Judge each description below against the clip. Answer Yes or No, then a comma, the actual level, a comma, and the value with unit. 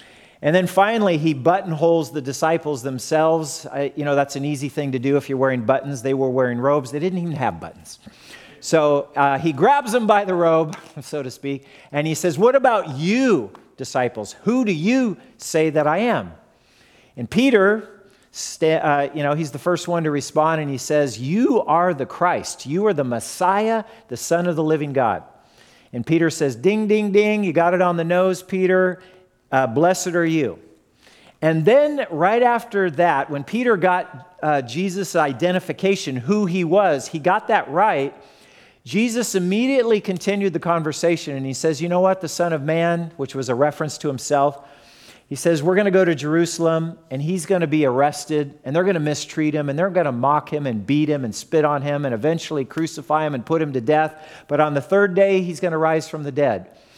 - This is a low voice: No, medium, 160 Hz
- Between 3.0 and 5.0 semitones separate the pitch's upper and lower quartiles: Yes, average, 4.4 semitones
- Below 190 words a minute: No, fast, 205 wpm